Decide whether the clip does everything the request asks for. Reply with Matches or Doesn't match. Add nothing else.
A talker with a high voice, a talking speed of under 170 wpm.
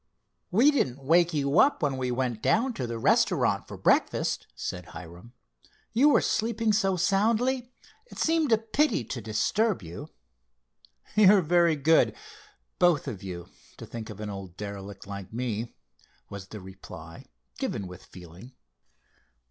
Doesn't match